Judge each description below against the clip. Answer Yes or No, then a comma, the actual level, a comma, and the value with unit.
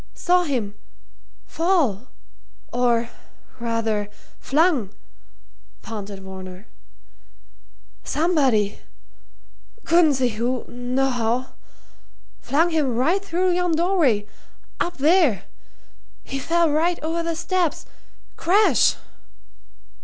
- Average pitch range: No, wide, 6.8 semitones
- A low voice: No, very high, 275 Hz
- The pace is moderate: No, slow, 85 wpm